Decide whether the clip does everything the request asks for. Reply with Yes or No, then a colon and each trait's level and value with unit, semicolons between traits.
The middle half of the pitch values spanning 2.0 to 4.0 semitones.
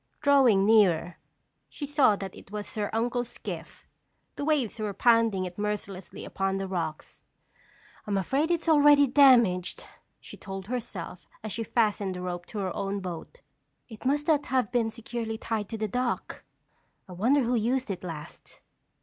No: average, 4.6 semitones